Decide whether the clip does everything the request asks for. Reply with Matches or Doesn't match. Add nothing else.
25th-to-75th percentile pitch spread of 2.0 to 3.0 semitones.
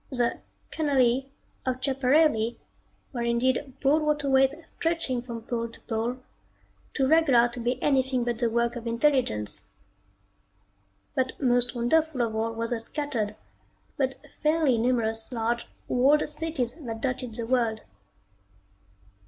Matches